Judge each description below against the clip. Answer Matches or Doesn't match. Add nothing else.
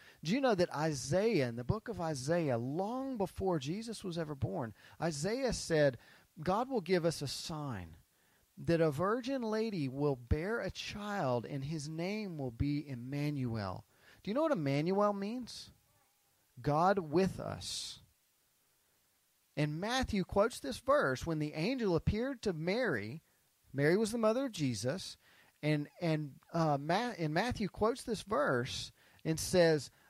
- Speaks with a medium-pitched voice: Matches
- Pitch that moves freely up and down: Matches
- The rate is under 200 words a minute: Matches